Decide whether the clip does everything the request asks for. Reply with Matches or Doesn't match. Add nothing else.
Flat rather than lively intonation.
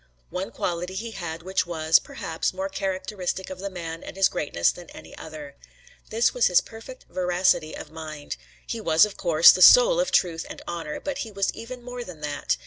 Doesn't match